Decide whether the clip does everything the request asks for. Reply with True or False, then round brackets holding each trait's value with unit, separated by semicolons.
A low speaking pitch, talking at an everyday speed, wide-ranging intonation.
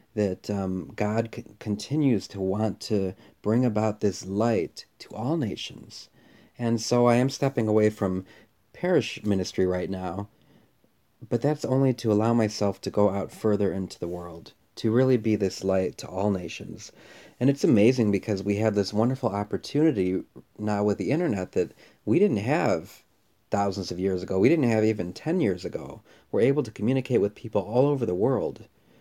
False (105 Hz; 175 wpm; 3.2 semitones)